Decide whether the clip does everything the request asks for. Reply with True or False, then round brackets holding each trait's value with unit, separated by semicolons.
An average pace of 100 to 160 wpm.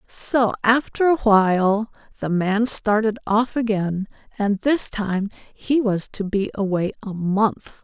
True (145 wpm)